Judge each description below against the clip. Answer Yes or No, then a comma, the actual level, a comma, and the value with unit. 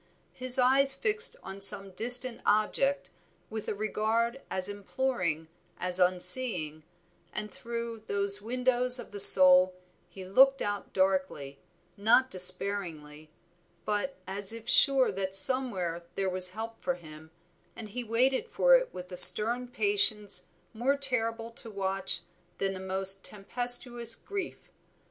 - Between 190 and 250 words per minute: No, slow, 135 wpm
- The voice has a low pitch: No, high, 210 Hz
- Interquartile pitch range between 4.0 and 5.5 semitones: Yes, average, 4.9 semitones